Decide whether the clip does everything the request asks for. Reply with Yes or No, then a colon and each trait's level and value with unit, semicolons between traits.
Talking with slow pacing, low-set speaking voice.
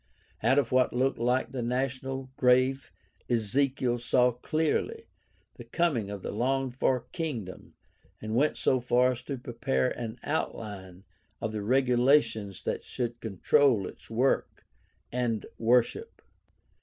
Yes: slow, 130 wpm; low, 125 Hz